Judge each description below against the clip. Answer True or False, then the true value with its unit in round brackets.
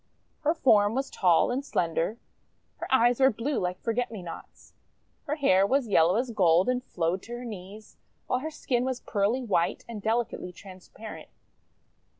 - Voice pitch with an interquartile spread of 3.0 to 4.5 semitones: False (5.2 semitones)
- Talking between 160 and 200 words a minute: True (165 wpm)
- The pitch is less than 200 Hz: False (225 Hz)